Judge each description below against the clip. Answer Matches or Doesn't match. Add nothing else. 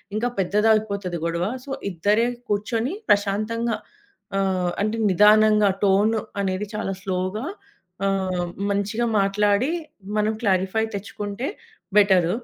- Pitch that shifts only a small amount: Matches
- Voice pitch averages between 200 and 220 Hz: Matches